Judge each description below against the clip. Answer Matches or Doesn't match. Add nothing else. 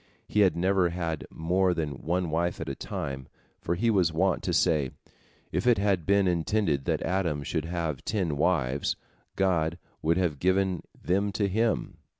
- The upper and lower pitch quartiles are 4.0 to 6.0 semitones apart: Doesn't match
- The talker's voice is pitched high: Doesn't match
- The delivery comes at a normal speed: Matches